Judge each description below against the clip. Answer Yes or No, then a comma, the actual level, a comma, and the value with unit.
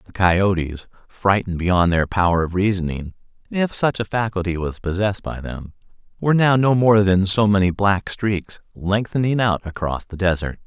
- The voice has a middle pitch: No, very low, 95 Hz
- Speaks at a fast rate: No, average, 170 wpm